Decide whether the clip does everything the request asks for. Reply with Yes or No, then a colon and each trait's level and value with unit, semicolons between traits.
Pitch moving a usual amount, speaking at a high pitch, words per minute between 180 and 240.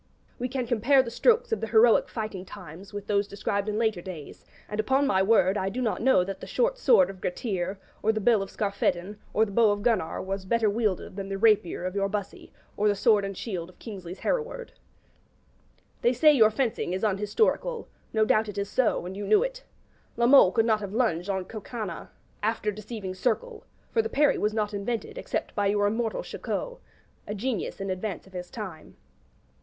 Yes: average, 3.3 semitones; high, 210 Hz; fast, 205 wpm